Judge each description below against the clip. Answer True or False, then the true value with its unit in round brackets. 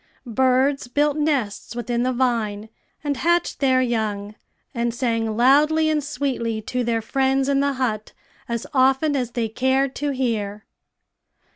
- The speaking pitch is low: False (255 Hz)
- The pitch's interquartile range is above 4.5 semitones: False (3.2 semitones)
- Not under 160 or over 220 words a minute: False (145 wpm)